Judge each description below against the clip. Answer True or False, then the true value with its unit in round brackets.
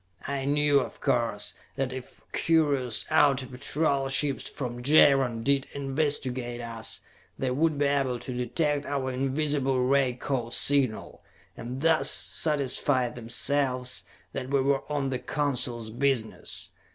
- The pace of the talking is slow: True (130 wpm)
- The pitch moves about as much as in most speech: False (2.3 semitones)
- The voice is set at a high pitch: False (135 Hz)